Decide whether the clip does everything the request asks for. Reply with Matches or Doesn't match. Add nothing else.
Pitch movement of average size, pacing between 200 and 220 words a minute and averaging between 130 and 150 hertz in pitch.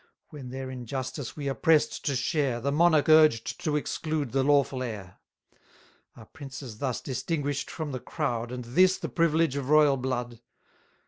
Doesn't match